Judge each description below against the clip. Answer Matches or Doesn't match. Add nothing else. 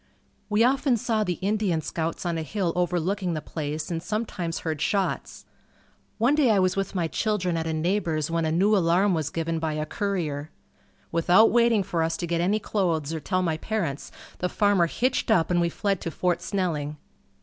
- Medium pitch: Matches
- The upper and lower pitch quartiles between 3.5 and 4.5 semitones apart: Matches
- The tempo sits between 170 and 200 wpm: Matches